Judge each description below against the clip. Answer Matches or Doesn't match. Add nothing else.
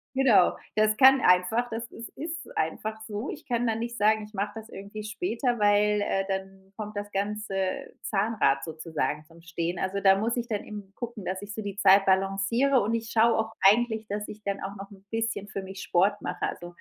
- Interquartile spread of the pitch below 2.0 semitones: Doesn't match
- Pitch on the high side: Matches